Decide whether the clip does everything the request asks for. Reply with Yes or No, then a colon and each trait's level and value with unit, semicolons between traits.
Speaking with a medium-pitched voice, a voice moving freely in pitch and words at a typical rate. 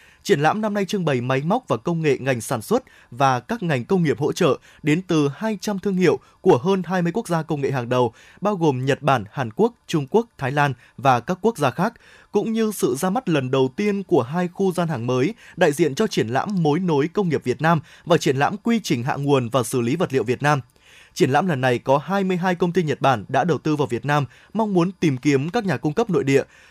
No: medium, 160 Hz; wide, 6.3 semitones; fast, 260 wpm